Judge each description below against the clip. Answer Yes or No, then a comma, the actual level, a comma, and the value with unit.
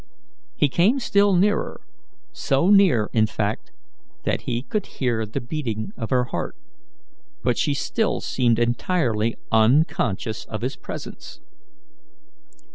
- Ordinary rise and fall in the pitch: No, wide, 7.3 semitones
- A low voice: Yes, low, 125 Hz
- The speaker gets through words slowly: Yes, slow, 120 wpm